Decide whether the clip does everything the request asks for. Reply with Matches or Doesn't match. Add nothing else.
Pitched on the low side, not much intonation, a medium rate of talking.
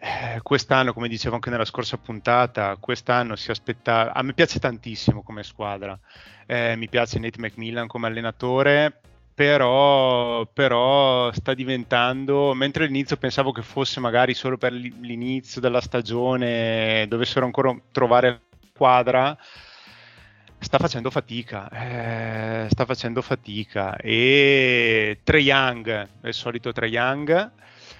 Matches